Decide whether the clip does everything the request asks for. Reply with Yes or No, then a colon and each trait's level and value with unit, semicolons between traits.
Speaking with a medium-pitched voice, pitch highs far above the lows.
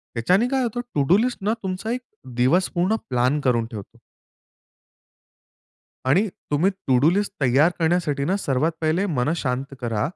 Yes: medium, 160 Hz; wide, 7.1 semitones